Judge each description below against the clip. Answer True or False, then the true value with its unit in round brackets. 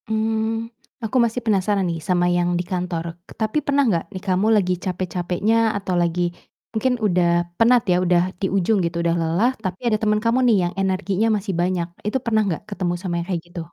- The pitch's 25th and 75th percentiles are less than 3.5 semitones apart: False (3.8 semitones)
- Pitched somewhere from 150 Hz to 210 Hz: True (190 Hz)